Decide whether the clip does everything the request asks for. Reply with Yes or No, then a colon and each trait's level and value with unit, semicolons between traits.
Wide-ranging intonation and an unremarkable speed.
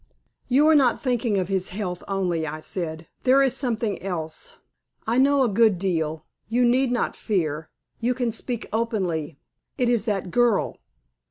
Yes: wide, 5.7 semitones; average, 165 wpm